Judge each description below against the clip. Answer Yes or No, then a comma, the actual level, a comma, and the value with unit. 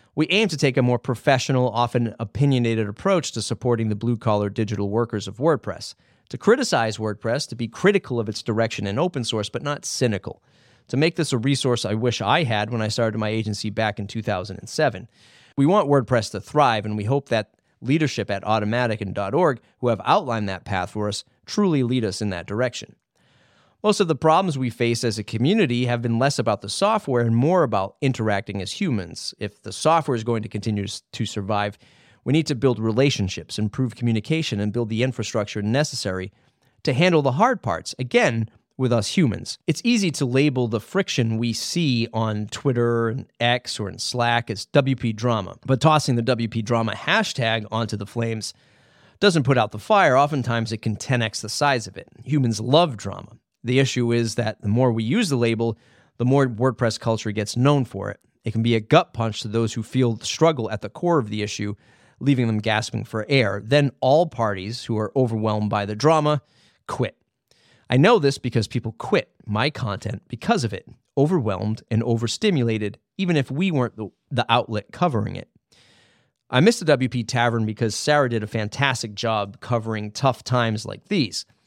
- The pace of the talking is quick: No, average, 190 wpm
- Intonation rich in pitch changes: No, average, 3.7 semitones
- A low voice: Yes, low, 120 Hz